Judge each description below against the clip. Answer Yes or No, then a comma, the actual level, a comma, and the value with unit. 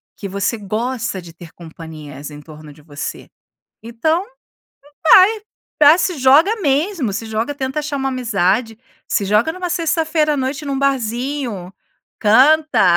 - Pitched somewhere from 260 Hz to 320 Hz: No, very high, 250 Hz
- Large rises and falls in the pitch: Yes, wide, 7.5 semitones